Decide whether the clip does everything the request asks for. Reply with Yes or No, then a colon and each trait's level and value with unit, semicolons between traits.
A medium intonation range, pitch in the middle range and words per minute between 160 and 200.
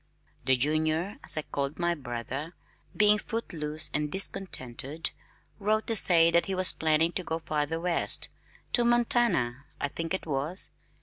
No: average, 4.3 semitones; medium, 165 Hz; average, 150 wpm